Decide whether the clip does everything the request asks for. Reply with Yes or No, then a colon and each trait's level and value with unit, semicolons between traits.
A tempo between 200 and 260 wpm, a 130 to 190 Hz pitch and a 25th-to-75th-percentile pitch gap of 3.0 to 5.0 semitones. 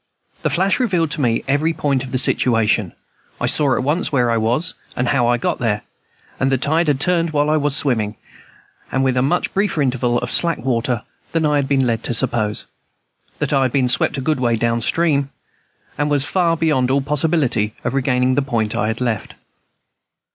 Yes: fast, 205 wpm; low, 135 Hz; average, 3.9 semitones